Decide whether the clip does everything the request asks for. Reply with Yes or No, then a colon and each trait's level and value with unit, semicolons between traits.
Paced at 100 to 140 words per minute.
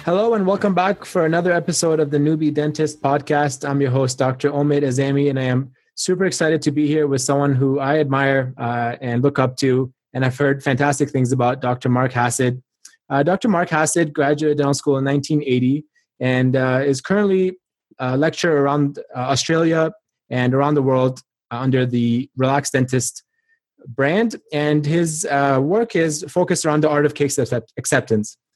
No: average, 180 wpm